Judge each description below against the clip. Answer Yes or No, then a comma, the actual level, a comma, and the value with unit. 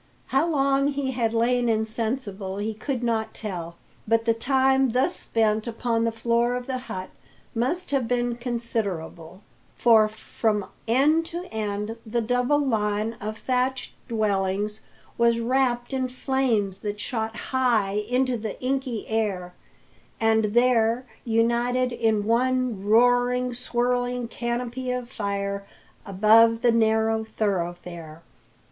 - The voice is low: No, high, 230 Hz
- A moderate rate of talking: No, slow, 125 wpm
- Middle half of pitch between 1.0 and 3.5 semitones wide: Yes, average, 2.7 semitones